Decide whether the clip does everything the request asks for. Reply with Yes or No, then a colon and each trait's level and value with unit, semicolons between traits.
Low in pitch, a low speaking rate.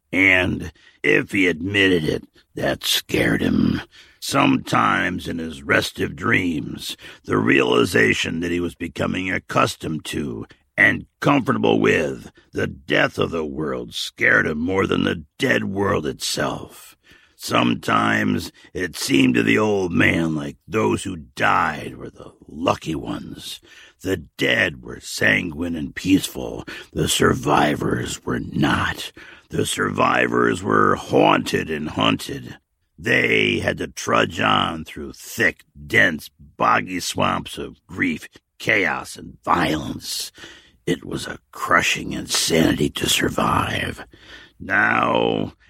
Yes: very low, 80 Hz; slow, 120 wpm